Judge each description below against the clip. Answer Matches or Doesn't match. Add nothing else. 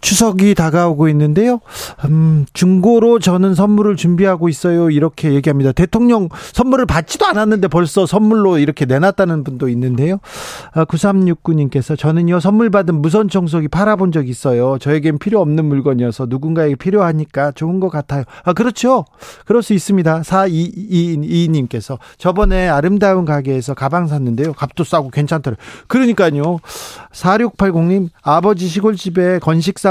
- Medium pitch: Matches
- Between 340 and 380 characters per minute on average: Matches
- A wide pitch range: Doesn't match